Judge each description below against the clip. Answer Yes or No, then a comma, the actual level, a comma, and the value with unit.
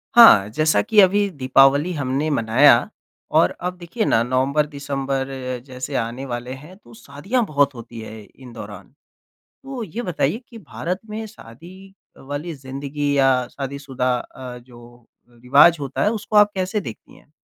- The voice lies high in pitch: No, medium, 140 Hz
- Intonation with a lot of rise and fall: Yes, wide, 6.1 semitones